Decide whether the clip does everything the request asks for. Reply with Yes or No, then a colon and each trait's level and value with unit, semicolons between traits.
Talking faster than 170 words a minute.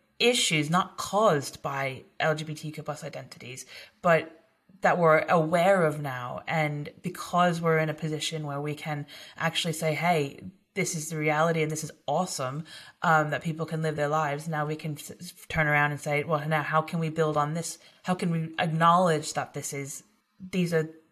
Yes: average, 180 wpm